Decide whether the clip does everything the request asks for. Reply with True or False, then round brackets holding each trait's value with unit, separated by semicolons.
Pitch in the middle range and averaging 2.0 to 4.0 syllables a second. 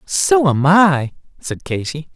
True (165 Hz; 3.4 syllables/s)